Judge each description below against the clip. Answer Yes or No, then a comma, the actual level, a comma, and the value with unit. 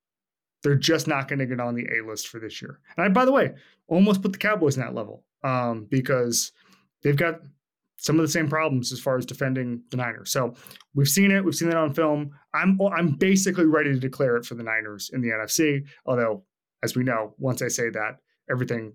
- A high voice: No, low, 135 Hz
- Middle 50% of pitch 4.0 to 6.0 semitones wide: Yes, average, 4.9 semitones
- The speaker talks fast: Yes, fast, 225 wpm